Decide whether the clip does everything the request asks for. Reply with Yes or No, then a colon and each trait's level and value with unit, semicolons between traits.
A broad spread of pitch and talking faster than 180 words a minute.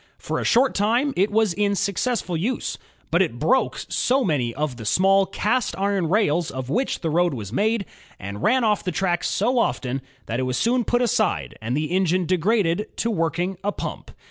Yes: wide, 5.7 semitones; average, 195 wpm